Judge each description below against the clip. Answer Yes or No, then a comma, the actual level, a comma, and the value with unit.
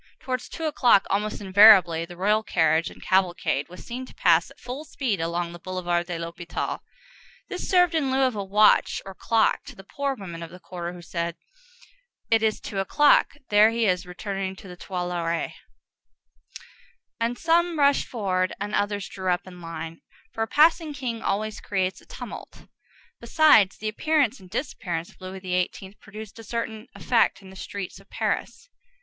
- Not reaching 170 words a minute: No, average, 180 wpm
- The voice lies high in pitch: Yes, high, 195 Hz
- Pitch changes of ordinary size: Yes, average, 4.6 semitones